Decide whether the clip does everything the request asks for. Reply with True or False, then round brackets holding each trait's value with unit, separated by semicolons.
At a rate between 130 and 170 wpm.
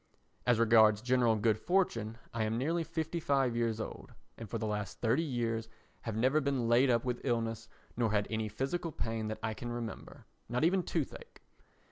False (185 wpm)